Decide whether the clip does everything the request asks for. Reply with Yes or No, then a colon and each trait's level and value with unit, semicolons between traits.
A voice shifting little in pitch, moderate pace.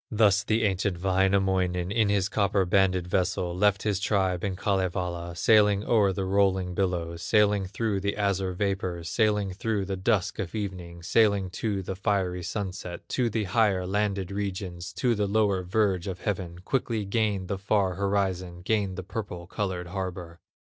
Yes: narrow, 2.1 semitones; average, 160 wpm